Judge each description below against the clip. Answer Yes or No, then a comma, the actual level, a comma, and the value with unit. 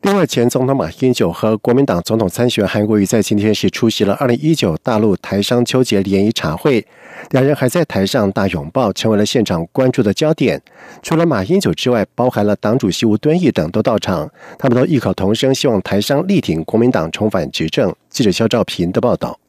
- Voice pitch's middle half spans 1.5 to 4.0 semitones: No, average, 4.8 semitones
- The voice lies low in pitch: Yes, low, 120 Hz